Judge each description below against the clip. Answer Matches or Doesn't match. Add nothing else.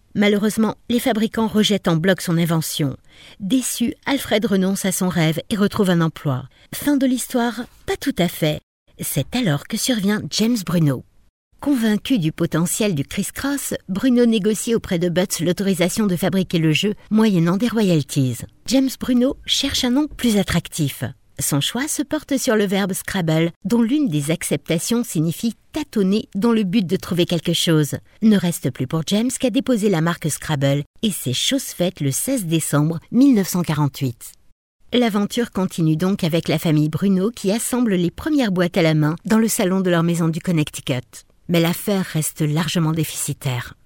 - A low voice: Doesn't match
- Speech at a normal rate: Matches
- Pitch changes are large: Matches